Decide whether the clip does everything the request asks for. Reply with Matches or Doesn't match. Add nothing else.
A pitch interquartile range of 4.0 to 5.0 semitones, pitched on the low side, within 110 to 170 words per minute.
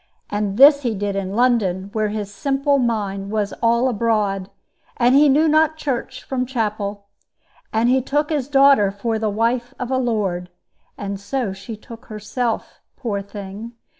Doesn't match